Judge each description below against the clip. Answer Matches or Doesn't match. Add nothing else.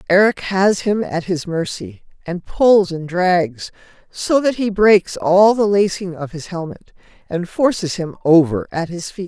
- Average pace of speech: Matches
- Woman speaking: Matches